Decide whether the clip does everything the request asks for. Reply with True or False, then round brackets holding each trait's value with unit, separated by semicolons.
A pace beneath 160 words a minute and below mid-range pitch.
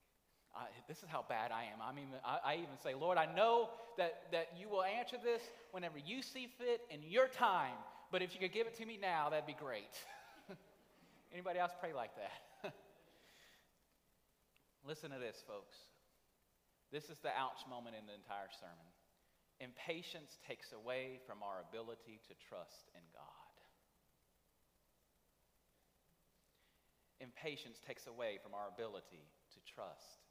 False (150 wpm; 165 Hz)